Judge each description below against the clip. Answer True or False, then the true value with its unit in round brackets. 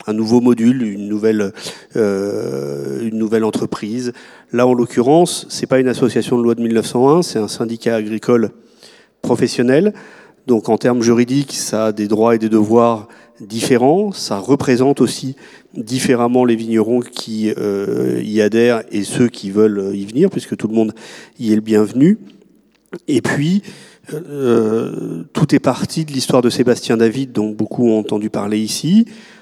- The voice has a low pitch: True (115 Hz)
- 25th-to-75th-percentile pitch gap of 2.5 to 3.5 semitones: True (3.0 semitones)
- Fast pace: False (160 wpm)